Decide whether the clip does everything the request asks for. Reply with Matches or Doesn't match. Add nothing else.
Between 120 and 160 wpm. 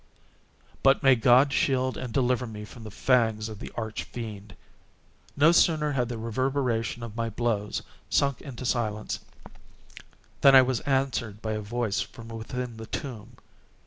Matches